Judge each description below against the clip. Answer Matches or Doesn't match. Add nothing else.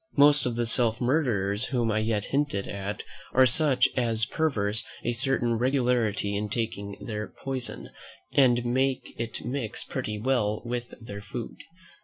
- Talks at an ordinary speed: Matches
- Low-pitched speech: Matches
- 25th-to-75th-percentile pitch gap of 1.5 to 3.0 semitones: Doesn't match